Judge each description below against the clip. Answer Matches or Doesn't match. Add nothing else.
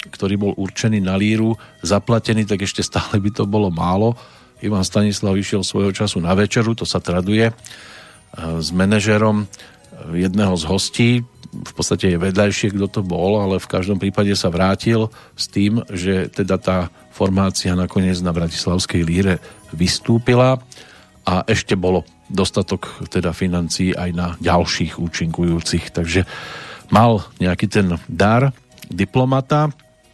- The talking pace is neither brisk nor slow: Matches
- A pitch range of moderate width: Matches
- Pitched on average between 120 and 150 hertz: Doesn't match